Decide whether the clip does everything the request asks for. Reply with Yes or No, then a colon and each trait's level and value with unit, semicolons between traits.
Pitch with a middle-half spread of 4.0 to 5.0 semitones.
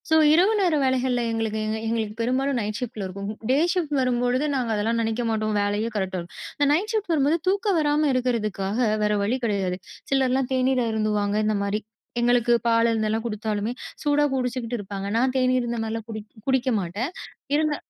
No: average, 3.6 semitones